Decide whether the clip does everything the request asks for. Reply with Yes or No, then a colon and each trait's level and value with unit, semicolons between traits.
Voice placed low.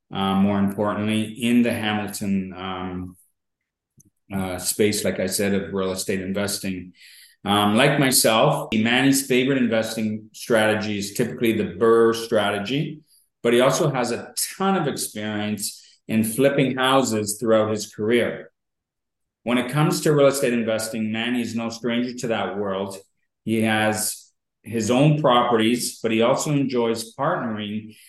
Yes: low, 110 Hz